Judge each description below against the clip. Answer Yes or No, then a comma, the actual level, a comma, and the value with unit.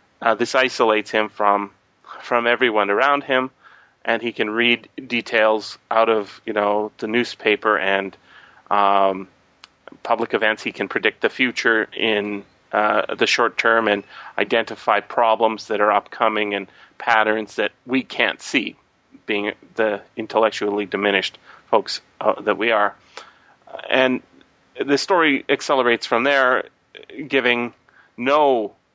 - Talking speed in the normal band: No, slow, 130 wpm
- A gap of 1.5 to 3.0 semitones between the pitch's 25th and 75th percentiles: Yes, narrow, 2.6 semitones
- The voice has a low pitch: Yes, low, 110 Hz